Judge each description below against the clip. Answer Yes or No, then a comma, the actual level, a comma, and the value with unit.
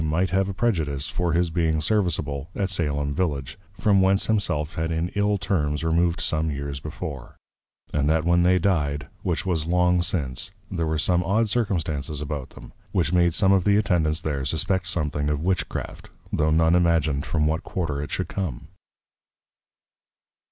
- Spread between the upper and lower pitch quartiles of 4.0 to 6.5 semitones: No, average, 3.6 semitones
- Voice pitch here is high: No, very low, 80 Hz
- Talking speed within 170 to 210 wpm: Yes, average, 175 wpm